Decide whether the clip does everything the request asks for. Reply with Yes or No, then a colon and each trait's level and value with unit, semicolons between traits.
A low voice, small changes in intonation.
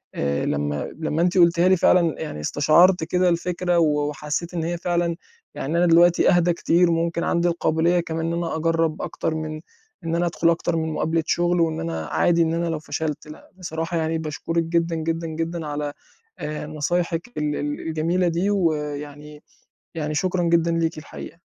No: medium, 165 Hz; narrow, 1.9 semitones